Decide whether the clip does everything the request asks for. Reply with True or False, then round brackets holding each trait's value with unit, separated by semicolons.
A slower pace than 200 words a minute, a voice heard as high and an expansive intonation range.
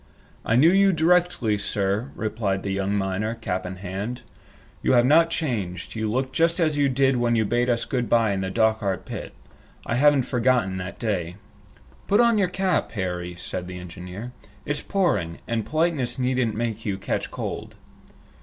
False (175 wpm; 115 Hz; 5.9 semitones)